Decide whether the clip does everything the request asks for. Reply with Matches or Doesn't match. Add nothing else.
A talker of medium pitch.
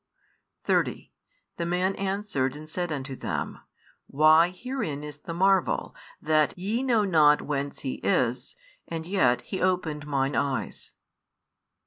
Matches